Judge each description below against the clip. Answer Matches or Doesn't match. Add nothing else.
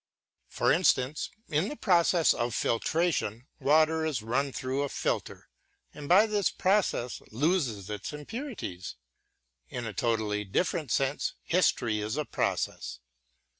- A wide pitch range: Matches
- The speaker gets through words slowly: Matches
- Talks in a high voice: Doesn't match